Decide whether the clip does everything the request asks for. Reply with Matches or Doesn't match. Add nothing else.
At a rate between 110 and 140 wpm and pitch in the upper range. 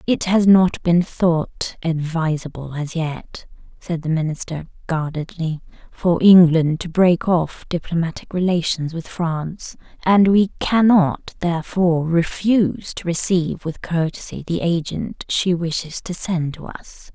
Doesn't match